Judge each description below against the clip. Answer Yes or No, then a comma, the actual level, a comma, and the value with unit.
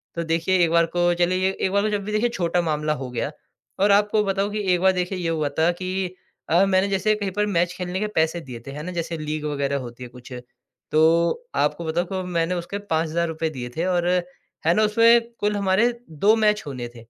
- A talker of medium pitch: Yes, medium, 175 Hz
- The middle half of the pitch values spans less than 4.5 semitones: Yes, average, 3.8 semitones